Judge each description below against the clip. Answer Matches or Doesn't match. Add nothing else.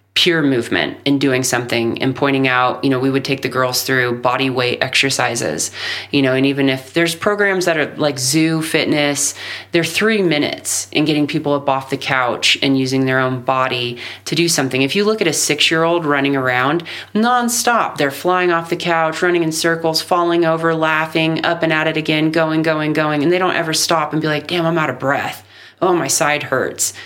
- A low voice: Doesn't match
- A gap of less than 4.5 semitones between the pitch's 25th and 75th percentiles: Matches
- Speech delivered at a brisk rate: Matches